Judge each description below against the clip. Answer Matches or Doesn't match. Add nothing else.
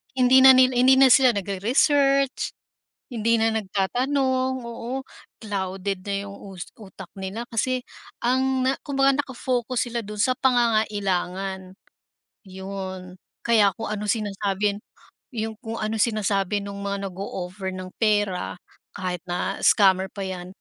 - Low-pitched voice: Doesn't match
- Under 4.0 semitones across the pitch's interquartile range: Doesn't match